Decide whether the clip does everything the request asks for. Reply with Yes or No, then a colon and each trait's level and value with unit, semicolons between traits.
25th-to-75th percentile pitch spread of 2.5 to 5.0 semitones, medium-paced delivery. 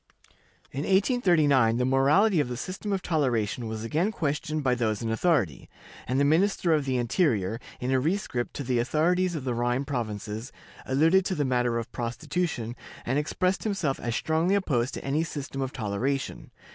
No: wide, 5.5 semitones; average, 175 wpm